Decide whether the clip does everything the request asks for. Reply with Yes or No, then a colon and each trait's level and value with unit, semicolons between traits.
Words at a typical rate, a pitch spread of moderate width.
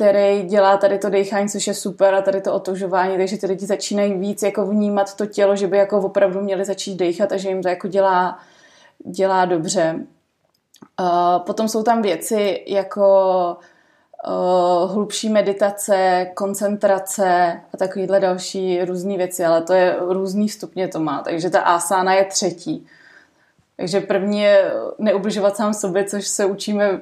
No: average, 160 wpm; narrow, 1.7 semitones